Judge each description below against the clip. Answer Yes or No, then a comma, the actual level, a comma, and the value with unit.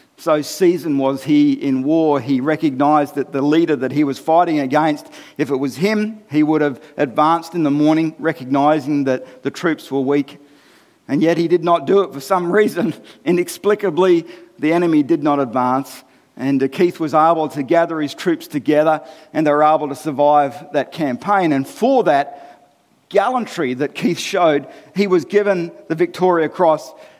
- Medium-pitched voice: Yes, medium, 155 Hz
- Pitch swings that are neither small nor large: Yes, average, 3.3 semitones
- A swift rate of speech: No, average, 175 wpm